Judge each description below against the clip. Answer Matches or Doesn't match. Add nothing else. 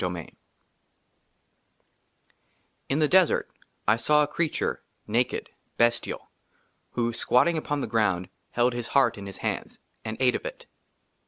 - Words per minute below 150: Matches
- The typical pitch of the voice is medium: Doesn't match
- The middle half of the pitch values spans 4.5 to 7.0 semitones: Matches